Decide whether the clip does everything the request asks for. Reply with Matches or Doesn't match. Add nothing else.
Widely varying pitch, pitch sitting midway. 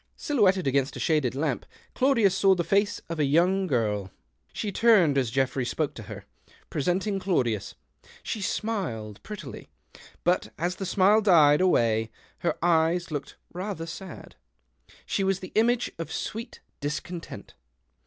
Matches